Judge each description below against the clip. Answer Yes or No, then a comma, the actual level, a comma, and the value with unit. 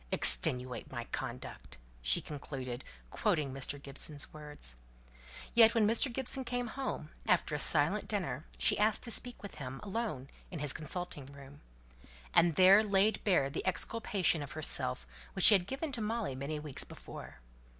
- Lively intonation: Yes, wide, 7.4 semitones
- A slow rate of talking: No, average, 160 wpm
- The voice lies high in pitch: No, medium, 165 Hz